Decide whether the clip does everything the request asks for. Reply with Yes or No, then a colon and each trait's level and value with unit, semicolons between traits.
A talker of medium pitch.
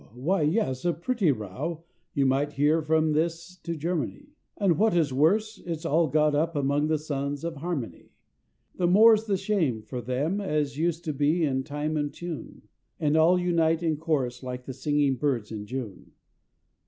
Yes: medium, 155 Hz